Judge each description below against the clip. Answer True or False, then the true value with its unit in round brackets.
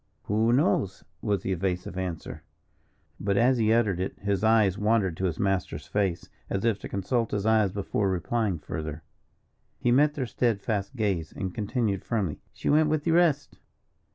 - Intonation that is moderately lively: True (3.6 semitones)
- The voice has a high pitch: False (105 Hz)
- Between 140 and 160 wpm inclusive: False (170 wpm)